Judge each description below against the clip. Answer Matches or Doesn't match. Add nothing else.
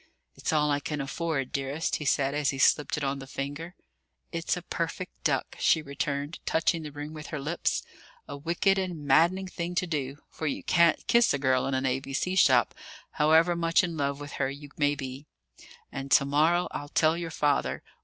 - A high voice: Doesn't match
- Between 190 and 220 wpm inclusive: Matches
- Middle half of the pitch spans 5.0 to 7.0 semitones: Doesn't match